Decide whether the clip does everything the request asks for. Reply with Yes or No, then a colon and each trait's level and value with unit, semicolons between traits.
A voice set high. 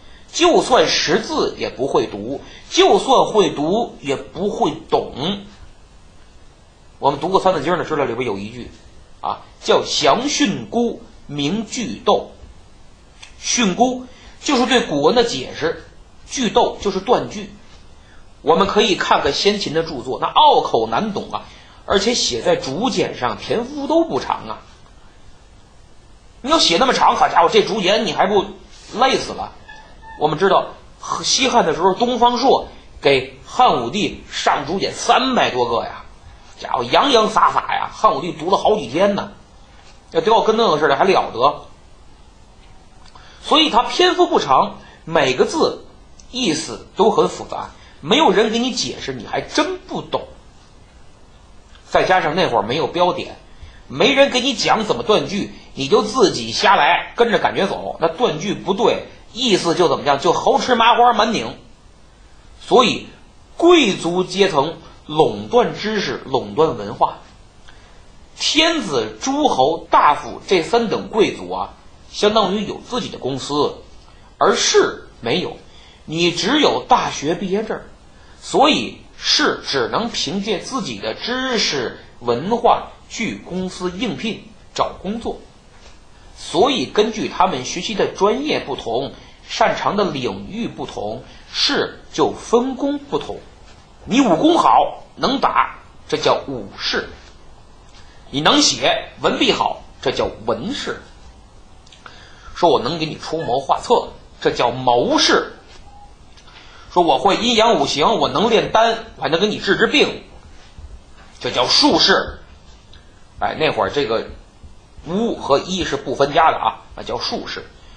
Yes: high, 225 Hz